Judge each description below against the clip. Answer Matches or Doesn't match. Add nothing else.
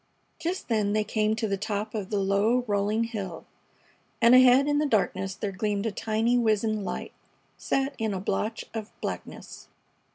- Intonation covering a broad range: Doesn't match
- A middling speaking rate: Matches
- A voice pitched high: Matches